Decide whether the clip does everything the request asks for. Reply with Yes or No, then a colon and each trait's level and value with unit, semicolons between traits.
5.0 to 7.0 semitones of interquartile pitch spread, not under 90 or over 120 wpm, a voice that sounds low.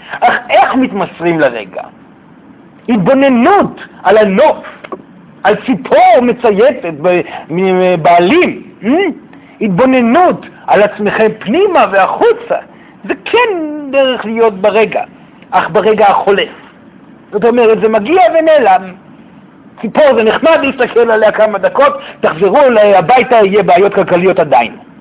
No: wide, 5.4 semitones; average, 105 wpm; high, 225 Hz